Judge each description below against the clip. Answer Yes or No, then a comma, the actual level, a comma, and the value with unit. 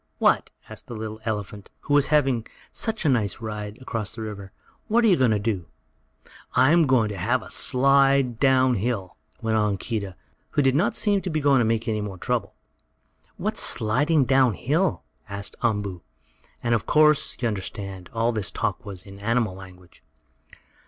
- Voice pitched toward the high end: No, low, 115 Hz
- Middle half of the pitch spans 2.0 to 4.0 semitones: No, average, 4.7 semitones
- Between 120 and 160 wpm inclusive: No, average, 180 wpm